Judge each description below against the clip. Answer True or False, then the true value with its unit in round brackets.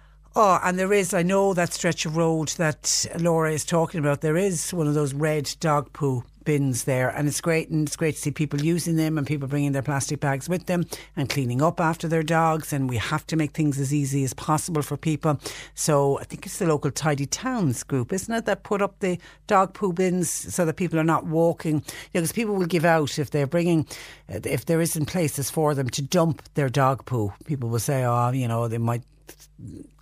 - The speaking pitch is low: False (155 Hz)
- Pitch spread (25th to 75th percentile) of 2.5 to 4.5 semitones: True (3.2 semitones)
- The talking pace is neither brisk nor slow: False (230 wpm)